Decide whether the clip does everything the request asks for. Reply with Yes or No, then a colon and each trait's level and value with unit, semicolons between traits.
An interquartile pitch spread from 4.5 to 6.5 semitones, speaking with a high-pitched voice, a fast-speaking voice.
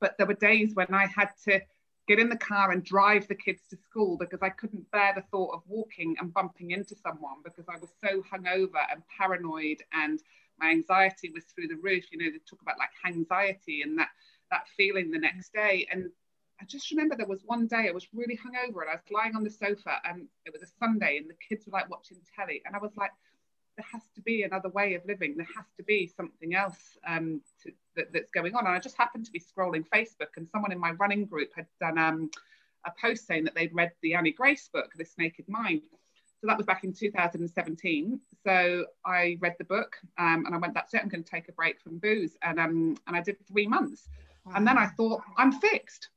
No: average, 4.1 semitones; high, 195 Hz; fast, 240 wpm